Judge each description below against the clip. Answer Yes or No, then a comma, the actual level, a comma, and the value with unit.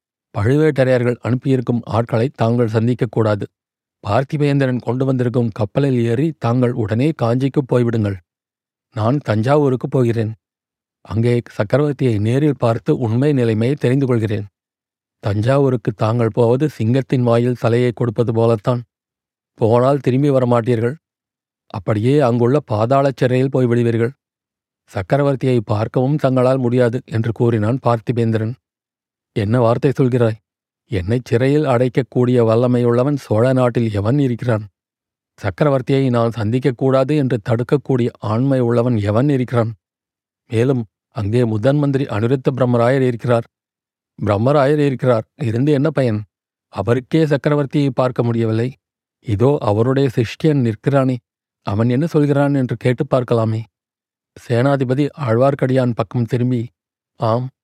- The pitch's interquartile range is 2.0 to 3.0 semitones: Yes, average, 2.7 semitones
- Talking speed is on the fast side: No, average, 105 wpm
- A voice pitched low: Yes, low, 125 Hz